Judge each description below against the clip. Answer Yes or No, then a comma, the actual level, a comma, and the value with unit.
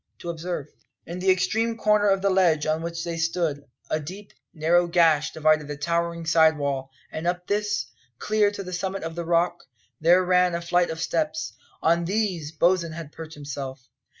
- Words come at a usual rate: Yes, average, 185 wpm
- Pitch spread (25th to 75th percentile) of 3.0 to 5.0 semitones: No, narrow, 2.4 semitones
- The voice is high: No, medium, 170 Hz